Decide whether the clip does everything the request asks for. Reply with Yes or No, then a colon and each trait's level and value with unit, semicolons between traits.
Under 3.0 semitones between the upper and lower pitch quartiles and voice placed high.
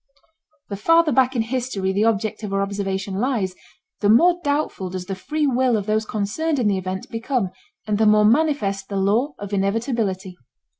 No: average, 4.7 semitones; high, 215 Hz